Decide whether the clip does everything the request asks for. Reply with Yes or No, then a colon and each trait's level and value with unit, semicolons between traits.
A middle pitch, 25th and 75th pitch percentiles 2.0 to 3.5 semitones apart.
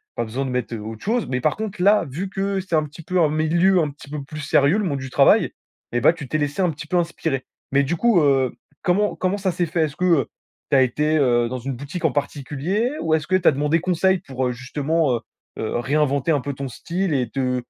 No: medium, 150 Hz; average, 4.8 semitones